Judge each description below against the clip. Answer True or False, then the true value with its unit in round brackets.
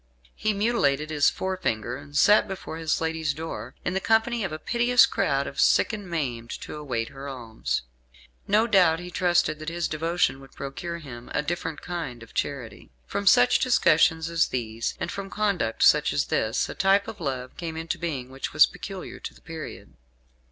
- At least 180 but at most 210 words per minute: True (185 wpm)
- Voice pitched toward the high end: False (160 Hz)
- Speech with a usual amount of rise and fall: False (5.8 semitones)